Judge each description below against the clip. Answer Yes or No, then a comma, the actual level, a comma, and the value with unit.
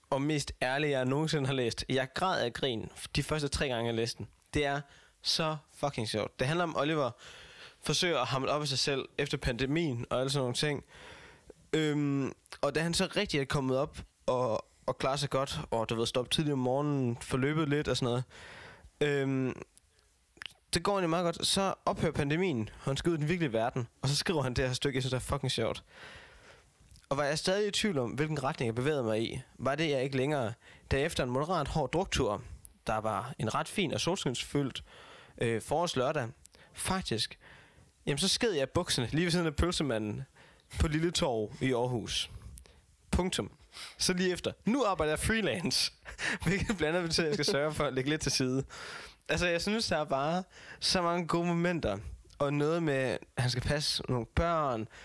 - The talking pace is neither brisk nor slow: Yes, average, 205 wpm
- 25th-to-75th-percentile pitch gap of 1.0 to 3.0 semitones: No, average, 3.6 semitones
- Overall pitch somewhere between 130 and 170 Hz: Yes, medium, 140 Hz